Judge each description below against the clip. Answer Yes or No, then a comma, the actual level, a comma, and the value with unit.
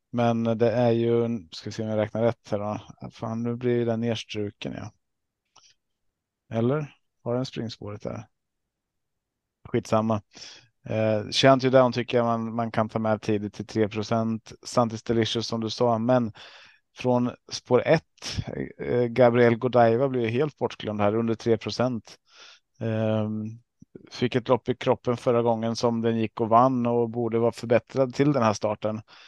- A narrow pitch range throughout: Yes, narrow, 1.8 semitones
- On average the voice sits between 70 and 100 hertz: No, low, 115 Hz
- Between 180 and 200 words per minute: No, average, 155 wpm